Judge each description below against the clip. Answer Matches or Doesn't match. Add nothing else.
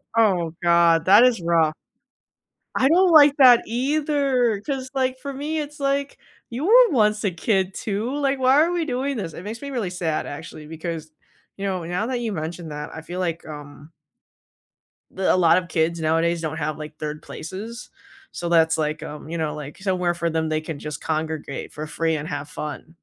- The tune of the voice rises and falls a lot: Matches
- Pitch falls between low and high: Matches